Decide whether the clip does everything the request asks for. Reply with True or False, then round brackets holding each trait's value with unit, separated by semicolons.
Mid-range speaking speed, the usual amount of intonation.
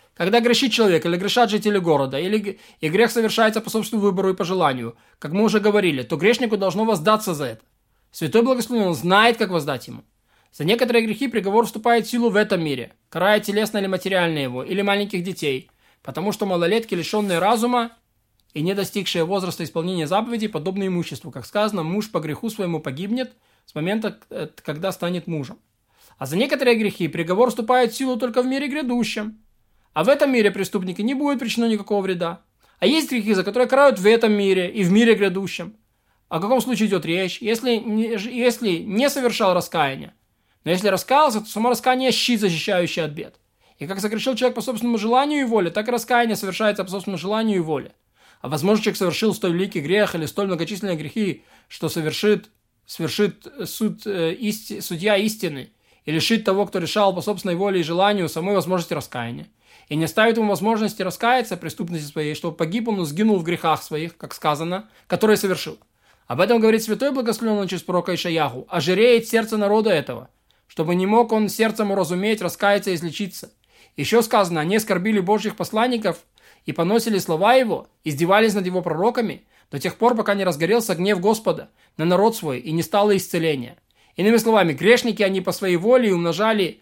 False (180 wpm; 4.5 semitones)